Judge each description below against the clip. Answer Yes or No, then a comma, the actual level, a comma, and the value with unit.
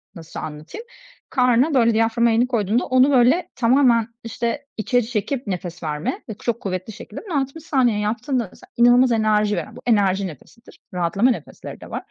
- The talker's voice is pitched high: Yes, high, 230 Hz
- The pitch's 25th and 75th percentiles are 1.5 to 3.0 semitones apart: No, average, 3.6 semitones